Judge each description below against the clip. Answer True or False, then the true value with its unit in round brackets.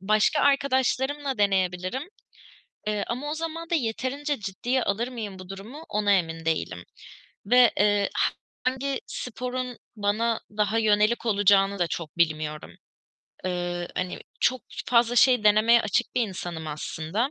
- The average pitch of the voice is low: False (215 Hz)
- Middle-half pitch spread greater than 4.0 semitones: True (5.1 semitones)